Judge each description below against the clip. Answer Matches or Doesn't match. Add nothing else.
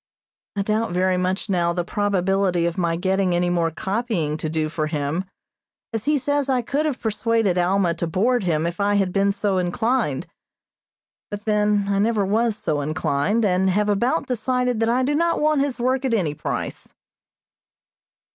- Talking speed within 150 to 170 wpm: Doesn't match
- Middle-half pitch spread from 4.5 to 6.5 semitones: Matches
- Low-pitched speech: Doesn't match